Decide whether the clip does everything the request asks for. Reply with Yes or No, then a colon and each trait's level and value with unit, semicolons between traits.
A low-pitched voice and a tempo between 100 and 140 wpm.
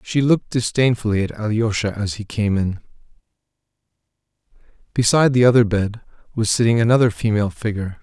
Yes: low, 110 Hz; slow, 135 wpm